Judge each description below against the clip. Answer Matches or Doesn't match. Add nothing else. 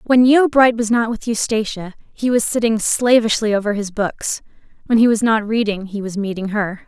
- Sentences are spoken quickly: Doesn't match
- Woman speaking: Matches